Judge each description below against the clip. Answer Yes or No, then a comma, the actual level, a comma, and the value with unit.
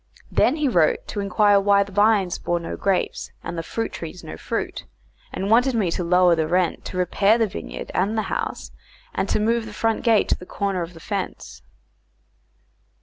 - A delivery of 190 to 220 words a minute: Yes, average, 200 wpm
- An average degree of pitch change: Yes, average, 3.5 semitones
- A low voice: No, high, 200 Hz